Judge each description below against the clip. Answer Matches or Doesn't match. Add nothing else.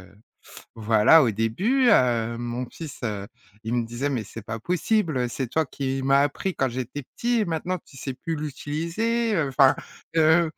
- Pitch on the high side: Doesn't match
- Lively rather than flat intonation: Matches